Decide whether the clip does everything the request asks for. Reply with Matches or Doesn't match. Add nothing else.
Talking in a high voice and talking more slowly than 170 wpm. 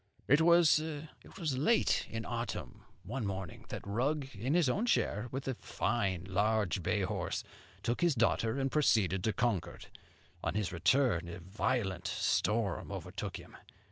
Doesn't match